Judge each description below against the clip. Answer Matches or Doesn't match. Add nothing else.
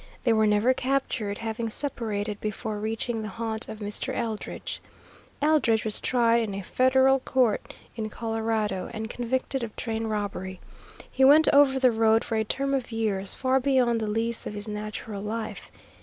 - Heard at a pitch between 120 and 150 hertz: Doesn't match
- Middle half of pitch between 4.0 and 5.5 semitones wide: Doesn't match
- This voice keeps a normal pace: Matches